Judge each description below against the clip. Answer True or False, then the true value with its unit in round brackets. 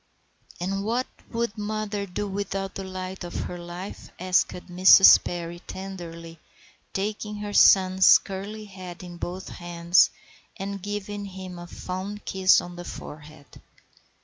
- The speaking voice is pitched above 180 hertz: True (190 Hz)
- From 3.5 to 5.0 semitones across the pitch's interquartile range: False (2.4 semitones)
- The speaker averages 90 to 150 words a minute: True (140 wpm)